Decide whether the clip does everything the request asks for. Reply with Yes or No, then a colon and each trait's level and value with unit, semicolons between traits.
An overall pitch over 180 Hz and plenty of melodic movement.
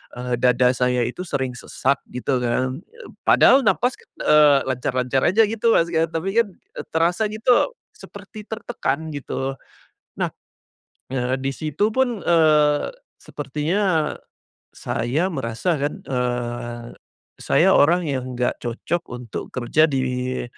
No: medium, 145 Hz; wide, 6.1 semitones